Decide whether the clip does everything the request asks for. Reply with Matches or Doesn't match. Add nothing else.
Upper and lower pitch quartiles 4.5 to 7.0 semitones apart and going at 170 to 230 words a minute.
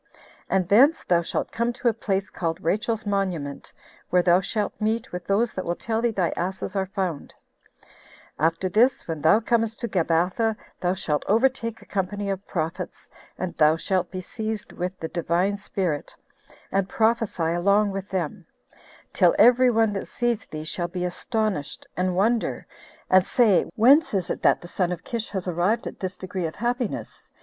Doesn't match